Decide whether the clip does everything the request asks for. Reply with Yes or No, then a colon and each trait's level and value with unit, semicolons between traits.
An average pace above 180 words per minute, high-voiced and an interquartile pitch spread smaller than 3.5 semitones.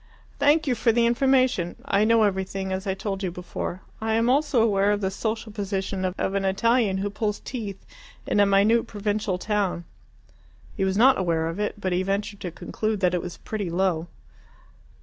Yes: average, 190 wpm; high, 200 Hz; average, 2.7 semitones